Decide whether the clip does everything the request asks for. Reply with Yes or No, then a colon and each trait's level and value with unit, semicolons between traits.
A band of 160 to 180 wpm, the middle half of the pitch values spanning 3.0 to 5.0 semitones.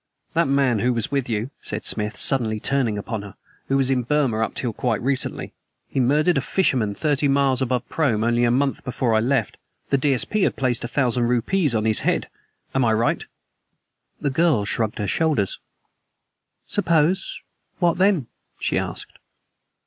Yes: average, 170 wpm; average, 3.7 semitones